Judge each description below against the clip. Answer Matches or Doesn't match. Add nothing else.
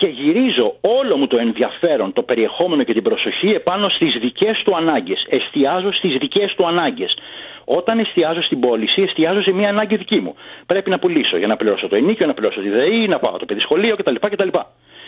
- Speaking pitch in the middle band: Doesn't match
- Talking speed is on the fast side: Matches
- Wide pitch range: Matches